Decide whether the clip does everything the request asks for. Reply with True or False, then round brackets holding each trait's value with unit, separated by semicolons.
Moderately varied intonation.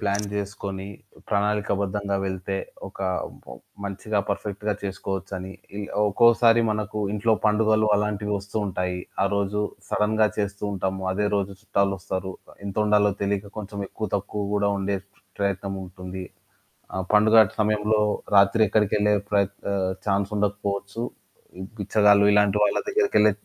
False (1.3 semitones)